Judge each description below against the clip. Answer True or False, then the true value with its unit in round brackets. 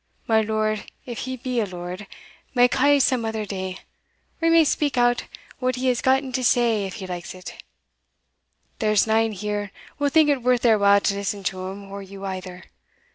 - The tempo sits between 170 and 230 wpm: True (195 wpm)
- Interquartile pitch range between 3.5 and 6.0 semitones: True (4.3 semitones)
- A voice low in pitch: False (220 Hz)